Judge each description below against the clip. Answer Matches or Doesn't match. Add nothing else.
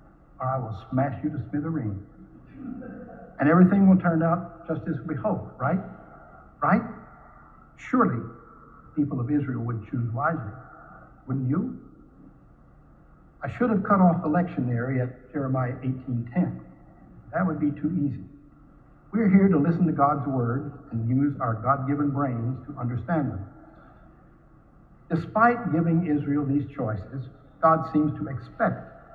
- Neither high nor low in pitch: Matches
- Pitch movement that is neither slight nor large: Matches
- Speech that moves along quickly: Doesn't match